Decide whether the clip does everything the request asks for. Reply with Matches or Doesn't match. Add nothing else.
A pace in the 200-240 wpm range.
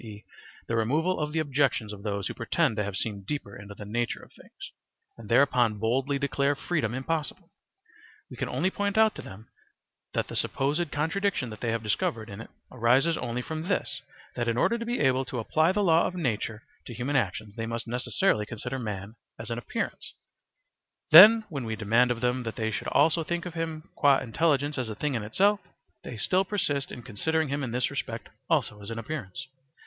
Matches